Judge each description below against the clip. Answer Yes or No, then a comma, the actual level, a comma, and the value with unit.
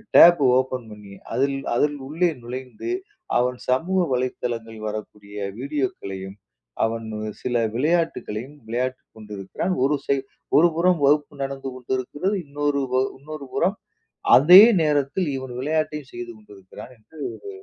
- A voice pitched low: Yes, low, 130 Hz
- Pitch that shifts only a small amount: No, average, 4.3 semitones